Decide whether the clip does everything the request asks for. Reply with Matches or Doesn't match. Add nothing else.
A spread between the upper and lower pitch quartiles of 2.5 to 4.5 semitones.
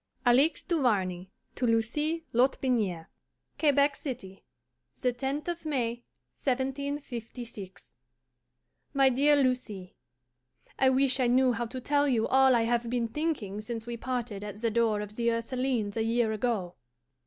Matches